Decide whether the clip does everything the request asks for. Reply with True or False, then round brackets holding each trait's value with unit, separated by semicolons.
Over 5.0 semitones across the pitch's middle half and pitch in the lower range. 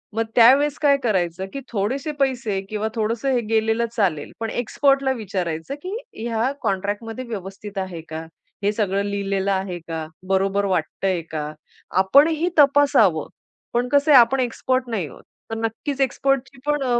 False (5.6 semitones; 225 Hz)